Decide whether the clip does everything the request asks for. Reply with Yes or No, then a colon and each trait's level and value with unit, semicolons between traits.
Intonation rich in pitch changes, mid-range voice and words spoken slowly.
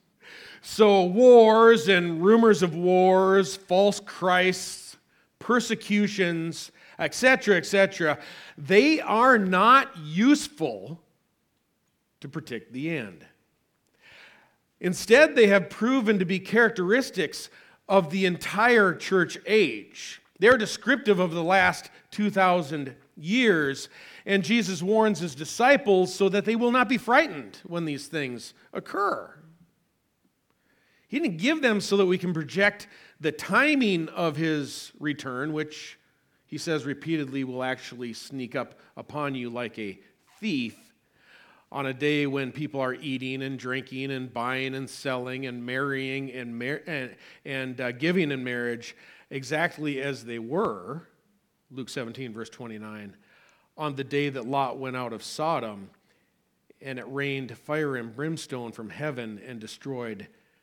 Yes: wide, 6.8 semitones; medium, 160 Hz; slow, 130 wpm